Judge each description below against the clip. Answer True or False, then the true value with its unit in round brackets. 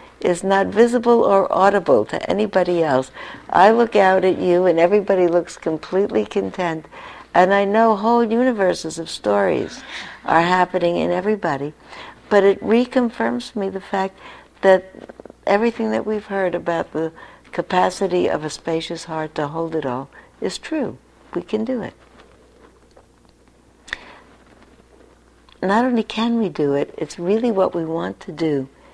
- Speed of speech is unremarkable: True (145 wpm)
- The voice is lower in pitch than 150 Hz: False (185 Hz)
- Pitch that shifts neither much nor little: True (4.5 semitones)